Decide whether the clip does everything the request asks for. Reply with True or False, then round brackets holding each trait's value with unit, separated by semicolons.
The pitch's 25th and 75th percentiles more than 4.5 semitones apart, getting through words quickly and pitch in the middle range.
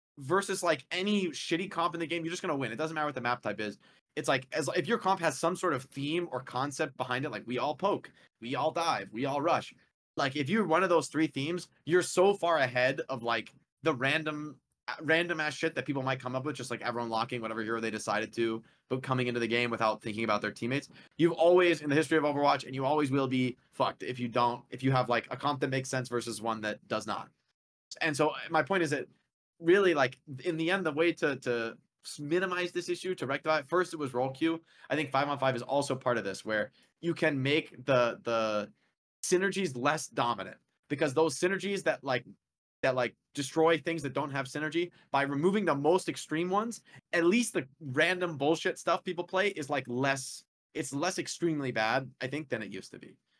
True (5.0 semitones; 230 wpm; 150 Hz)